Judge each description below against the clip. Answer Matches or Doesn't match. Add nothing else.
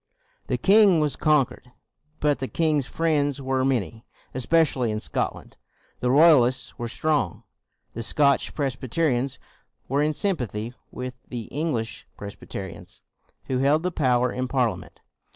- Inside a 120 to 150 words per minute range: Matches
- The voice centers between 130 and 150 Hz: Matches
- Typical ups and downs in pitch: Matches